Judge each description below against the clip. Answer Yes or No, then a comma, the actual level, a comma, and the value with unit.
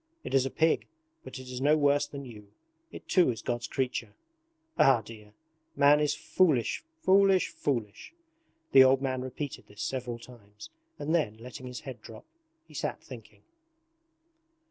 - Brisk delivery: No, average, 160 wpm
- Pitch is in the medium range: No, low, 130 Hz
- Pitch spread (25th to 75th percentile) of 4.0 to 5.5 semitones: No, average, 3.6 semitones